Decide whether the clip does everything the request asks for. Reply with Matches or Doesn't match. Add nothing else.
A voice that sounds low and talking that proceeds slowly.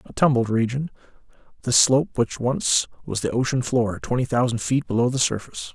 Doesn't match